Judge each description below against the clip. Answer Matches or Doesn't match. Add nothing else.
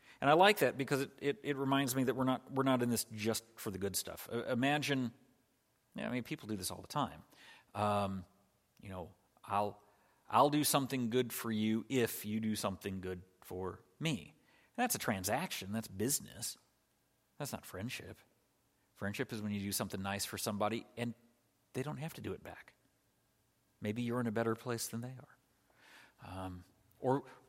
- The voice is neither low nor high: Doesn't match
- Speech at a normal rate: Matches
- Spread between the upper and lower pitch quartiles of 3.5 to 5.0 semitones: Matches